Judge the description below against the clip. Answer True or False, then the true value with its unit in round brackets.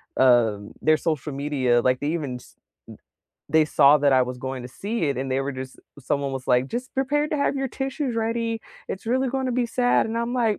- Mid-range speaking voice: True (155 Hz)